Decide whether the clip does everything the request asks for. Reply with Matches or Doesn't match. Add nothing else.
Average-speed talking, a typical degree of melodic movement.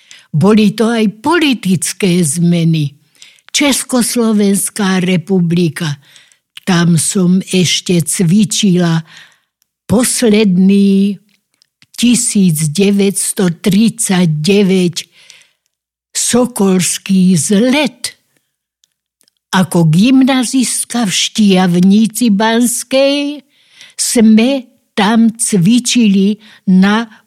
Doesn't match